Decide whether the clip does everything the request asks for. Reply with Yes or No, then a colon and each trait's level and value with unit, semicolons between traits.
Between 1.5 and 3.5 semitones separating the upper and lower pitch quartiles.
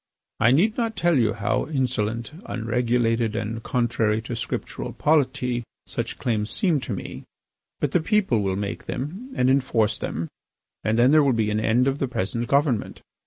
No: average, 4.0 semitones